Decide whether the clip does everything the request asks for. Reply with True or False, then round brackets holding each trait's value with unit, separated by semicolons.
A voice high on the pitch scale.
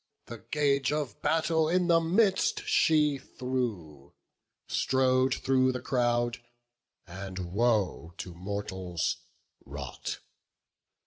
False (125 Hz)